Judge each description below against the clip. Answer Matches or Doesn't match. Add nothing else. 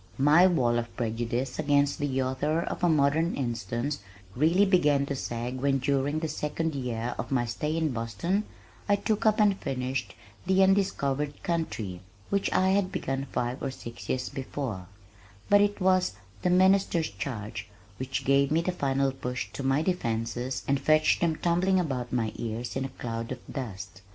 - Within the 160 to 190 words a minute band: Matches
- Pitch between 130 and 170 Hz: Matches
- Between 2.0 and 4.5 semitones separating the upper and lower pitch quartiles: Doesn't match